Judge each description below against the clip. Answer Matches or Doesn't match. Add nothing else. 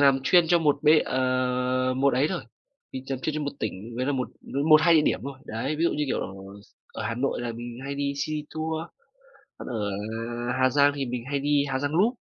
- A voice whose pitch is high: Doesn't match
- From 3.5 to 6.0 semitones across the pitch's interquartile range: Doesn't match